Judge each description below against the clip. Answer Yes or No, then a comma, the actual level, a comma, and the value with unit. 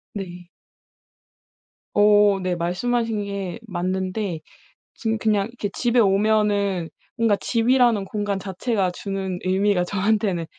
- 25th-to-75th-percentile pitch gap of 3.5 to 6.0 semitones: No, average, 2.7 semitones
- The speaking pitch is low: No, high, 200 Hz